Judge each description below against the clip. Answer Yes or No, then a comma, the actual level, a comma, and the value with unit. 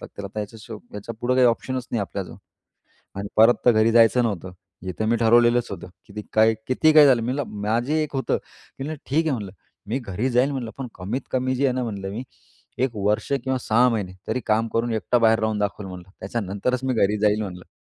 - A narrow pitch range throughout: No, average, 3.5 semitones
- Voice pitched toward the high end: No, low, 115 Hz